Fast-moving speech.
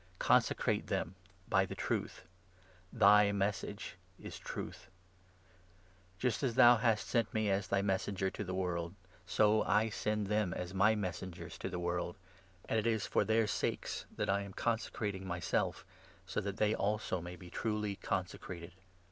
No: average, 165 wpm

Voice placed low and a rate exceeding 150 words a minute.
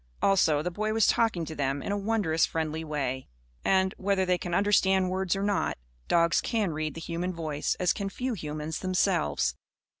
No: medium, 180 Hz; average, 185 wpm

